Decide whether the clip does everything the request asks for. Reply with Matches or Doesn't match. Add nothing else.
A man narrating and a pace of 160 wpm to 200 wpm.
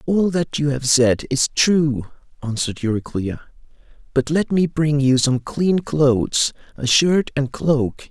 Doesn't match